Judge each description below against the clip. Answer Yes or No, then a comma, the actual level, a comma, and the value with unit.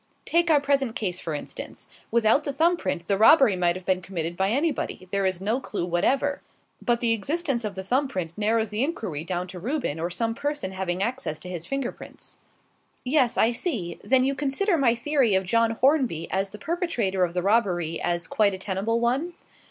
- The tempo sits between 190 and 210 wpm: Yes, fast, 205 wpm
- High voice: Yes, high, 225 Hz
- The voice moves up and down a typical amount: No, wide, 6.7 semitones